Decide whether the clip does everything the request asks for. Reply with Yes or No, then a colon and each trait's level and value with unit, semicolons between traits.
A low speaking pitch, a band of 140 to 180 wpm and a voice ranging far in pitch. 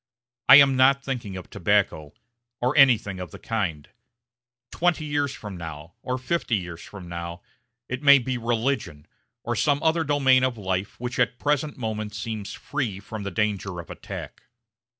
Yes: low, 115 Hz; average, 170 wpm; wide, 6.3 semitones